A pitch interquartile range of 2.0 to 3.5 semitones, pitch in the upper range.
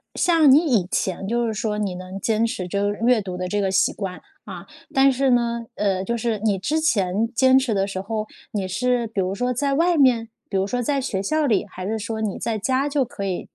No: average, 4.4 semitones; high, 220 Hz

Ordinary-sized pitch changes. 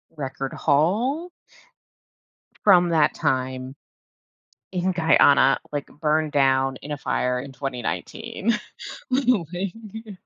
No: wide, 6.5 semitones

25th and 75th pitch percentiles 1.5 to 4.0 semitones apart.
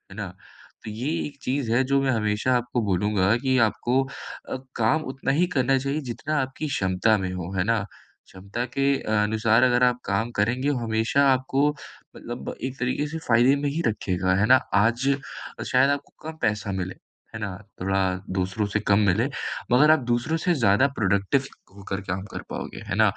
No: average, 4.8 semitones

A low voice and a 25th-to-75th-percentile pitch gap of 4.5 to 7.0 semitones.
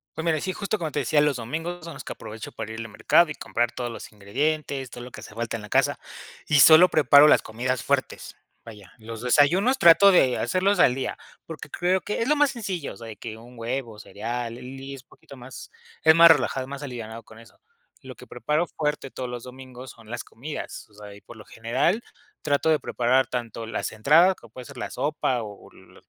Yes: low, 130 Hz; wide, 5.4 semitones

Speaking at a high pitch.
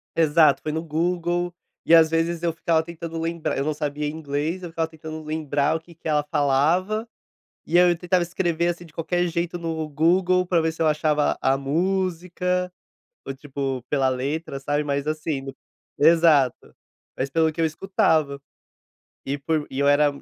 No: medium, 160 Hz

